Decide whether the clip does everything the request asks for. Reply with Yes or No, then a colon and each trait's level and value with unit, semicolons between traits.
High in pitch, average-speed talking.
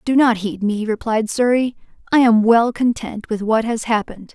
Yes: high, 225 Hz; average, 195 wpm